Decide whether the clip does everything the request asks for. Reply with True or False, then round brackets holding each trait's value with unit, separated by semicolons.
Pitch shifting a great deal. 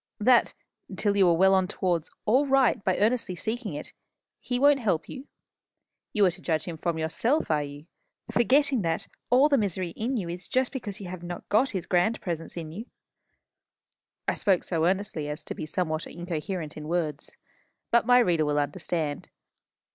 True (5.9 semitones)